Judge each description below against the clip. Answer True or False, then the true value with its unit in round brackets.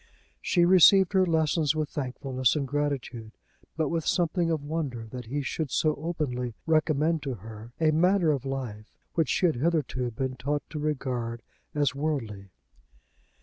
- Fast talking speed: False (155 wpm)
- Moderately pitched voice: True (145 Hz)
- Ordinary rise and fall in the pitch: True (4.2 semitones)